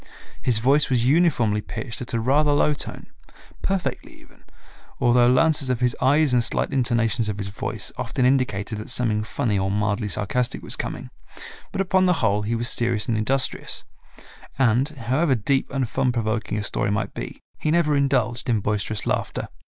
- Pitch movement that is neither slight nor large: Yes, average, 3.9 semitones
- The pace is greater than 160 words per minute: Yes, average, 175 wpm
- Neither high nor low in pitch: No, low, 120 Hz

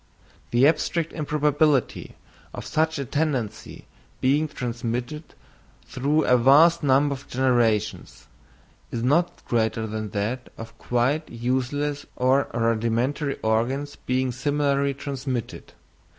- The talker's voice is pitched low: Yes, low, 130 Hz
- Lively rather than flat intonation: No, average, 3.6 semitones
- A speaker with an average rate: No, slow, 105 wpm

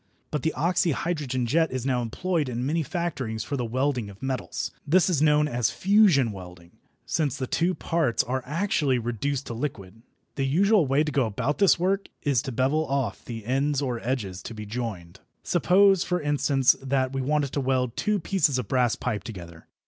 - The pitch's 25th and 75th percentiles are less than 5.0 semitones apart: Yes, average, 4.6 semitones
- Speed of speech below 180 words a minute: No, average, 190 wpm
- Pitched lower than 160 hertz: Yes, low, 135 Hz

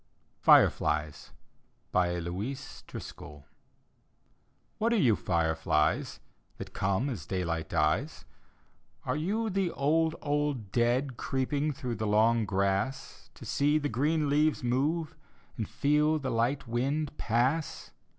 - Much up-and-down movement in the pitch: Yes, wide, 7.3 semitones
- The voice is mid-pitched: No, low, 130 Hz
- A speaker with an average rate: No, slow, 115 wpm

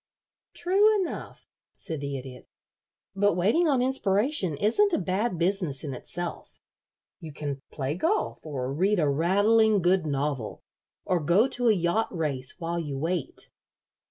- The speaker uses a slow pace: No, average, 145 wpm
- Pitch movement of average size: No, wide, 6.6 semitones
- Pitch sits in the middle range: Yes, medium, 175 Hz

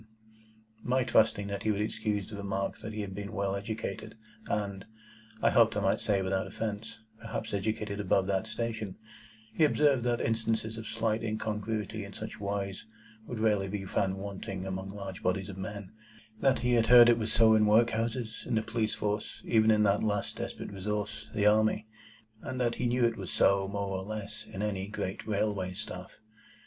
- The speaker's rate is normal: Yes, average, 190 wpm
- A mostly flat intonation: Yes, narrow, 2.1 semitones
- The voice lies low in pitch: Yes, low, 105 Hz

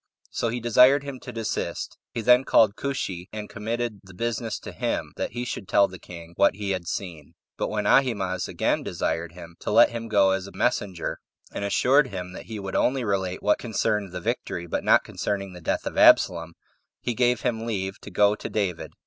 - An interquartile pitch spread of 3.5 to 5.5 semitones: Yes, average, 4.1 semitones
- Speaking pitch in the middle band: No, low, 105 Hz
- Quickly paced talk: Yes, fast, 210 wpm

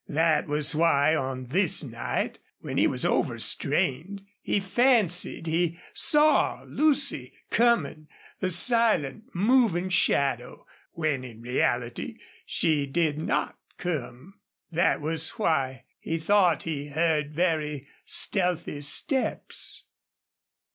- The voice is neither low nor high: Yes, medium, 160 Hz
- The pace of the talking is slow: Yes, slow, 105 wpm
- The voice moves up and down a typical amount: Yes, average, 4.8 semitones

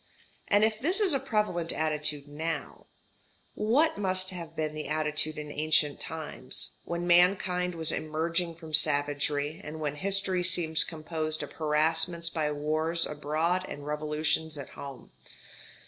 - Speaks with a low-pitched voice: No, medium, 160 Hz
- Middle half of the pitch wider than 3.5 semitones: No, average, 2.9 semitones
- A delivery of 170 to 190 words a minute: No, average, 140 wpm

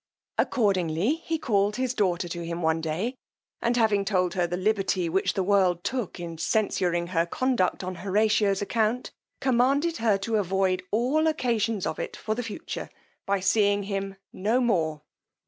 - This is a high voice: Yes, high, 200 Hz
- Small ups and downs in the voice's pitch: No, average, 4.2 semitones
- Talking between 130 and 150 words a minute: No, average, 165 wpm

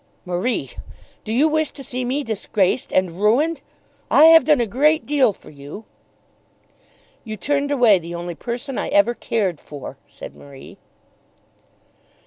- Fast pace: No, average, 145 wpm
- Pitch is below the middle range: No, high, 235 Hz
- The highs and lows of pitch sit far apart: Yes, wide, 7.4 semitones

